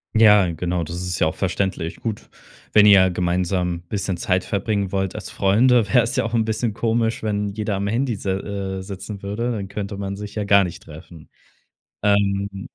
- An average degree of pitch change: No, narrow, 2.2 semitones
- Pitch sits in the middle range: No, low, 100 Hz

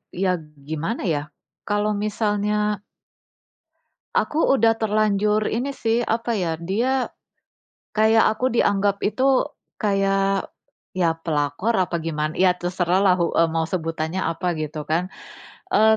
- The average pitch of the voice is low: No, high, 195 Hz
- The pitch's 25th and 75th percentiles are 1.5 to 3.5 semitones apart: No, average, 4.3 semitones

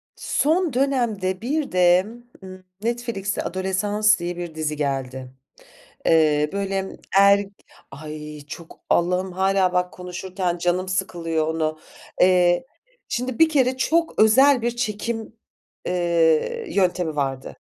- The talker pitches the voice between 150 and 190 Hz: Yes, medium, 185 Hz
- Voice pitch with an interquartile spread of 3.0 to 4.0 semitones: No, average, 4.8 semitones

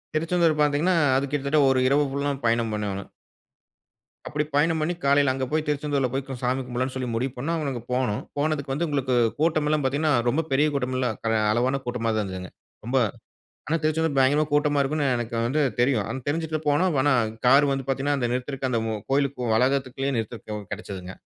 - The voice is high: No, low, 135 Hz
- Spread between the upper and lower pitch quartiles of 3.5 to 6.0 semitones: No, average, 2.9 semitones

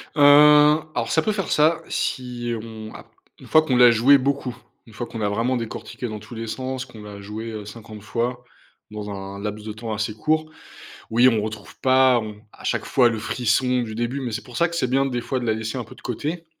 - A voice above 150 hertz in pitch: No, low, 120 Hz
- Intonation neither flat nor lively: Yes, average, 3.2 semitones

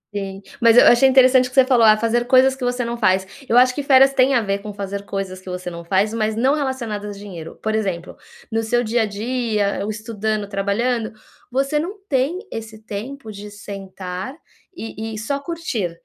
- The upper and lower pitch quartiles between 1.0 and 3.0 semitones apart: No, average, 4.2 semitones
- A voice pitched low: No, high, 220 Hz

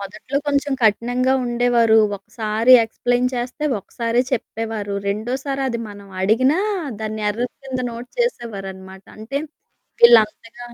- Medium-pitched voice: No, high, 235 Hz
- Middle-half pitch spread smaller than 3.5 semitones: Yes, average, 2.8 semitones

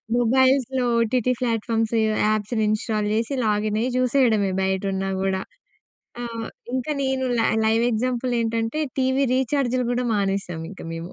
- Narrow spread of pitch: No, average, 3.3 semitones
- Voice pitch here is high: Yes, high, 230 Hz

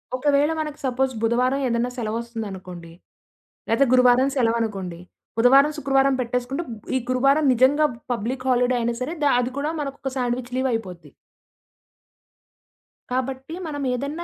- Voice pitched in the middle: No, very high, 255 Hz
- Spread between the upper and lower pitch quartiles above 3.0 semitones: No, average, 2.7 semitones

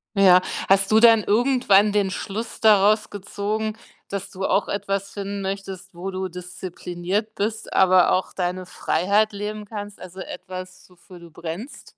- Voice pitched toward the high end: Yes, high, 195 Hz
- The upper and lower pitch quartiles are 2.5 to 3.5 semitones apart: No, narrow, 2.1 semitones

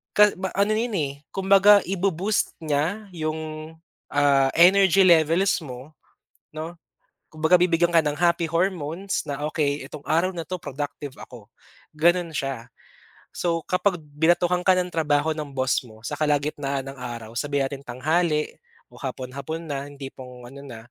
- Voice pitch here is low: No, medium, 155 Hz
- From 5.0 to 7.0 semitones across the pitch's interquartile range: No, average, 3.9 semitones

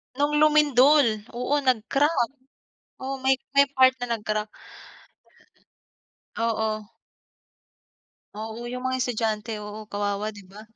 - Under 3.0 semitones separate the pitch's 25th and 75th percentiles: No, average, 3.6 semitones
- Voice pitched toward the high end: Yes, high, 235 Hz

